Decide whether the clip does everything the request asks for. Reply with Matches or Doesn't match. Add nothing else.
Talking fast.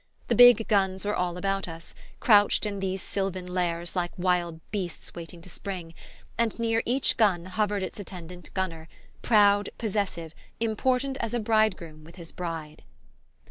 Doesn't match